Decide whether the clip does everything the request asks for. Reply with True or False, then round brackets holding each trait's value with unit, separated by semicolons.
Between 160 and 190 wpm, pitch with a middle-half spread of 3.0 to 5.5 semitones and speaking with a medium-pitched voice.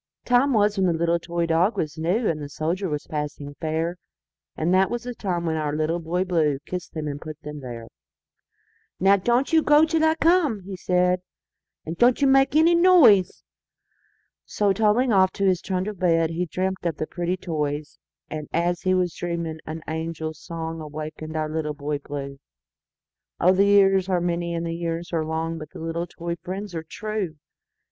True (165 wpm; 3.6 semitones; 170 Hz)